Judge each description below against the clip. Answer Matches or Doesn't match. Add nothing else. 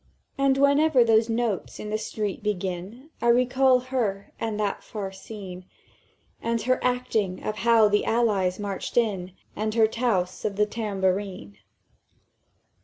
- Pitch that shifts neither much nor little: Matches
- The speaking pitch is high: Matches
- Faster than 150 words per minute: Doesn't match